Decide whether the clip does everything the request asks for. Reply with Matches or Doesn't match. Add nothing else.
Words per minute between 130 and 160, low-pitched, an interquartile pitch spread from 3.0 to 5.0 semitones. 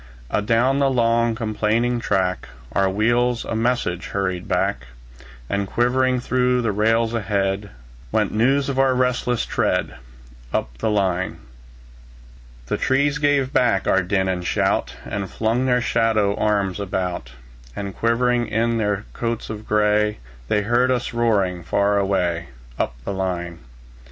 Matches